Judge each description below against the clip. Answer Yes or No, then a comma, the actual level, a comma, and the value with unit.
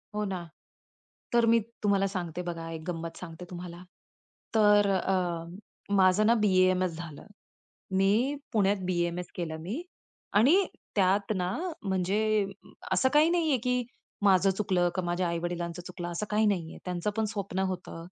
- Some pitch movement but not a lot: Yes, average, 3.2 semitones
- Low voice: No, medium, 185 Hz